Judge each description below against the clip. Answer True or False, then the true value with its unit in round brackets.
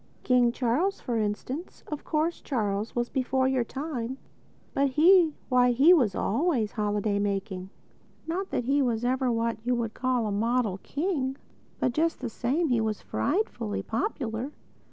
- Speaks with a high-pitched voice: True (250 Hz)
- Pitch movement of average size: True (4.2 semitones)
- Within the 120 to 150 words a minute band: True (145 wpm)